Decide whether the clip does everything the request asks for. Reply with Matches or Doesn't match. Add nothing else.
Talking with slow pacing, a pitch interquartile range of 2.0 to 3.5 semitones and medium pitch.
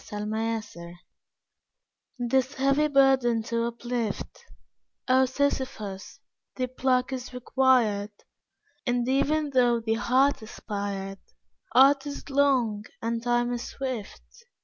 Doesn't match